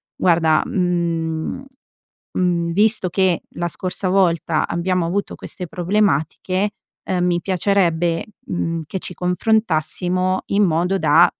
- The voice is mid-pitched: Yes, medium, 180 Hz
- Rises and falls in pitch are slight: Yes, narrow, 2.1 semitones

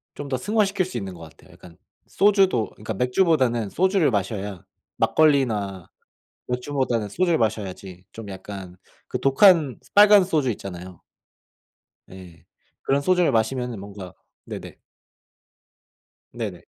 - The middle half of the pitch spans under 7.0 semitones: No, wide, 8.1 semitones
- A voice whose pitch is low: Yes, low, 120 Hz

